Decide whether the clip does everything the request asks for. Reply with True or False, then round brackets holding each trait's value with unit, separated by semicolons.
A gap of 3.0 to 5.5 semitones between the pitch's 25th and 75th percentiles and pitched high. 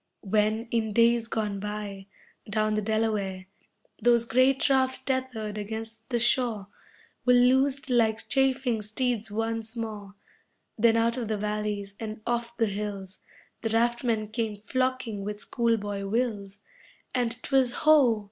False (2.4 semitones; 225 Hz)